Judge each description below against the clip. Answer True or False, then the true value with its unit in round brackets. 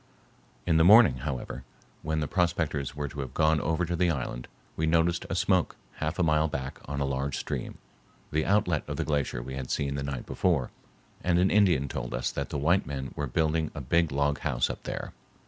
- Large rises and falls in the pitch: False (3.4 semitones)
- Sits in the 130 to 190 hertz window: False (75 Hz)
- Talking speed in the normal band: False (215 wpm)